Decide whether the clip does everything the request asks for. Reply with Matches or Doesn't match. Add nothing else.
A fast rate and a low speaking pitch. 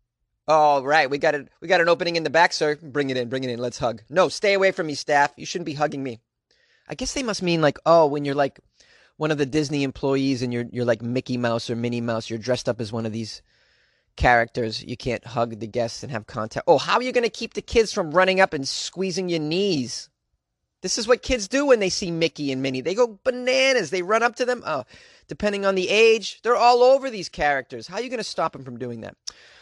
Doesn't match